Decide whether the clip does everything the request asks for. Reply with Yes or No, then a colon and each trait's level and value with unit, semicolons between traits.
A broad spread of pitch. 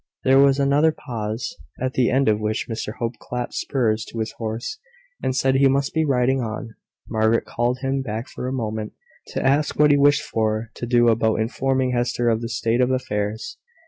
No: average, 3.1 semitones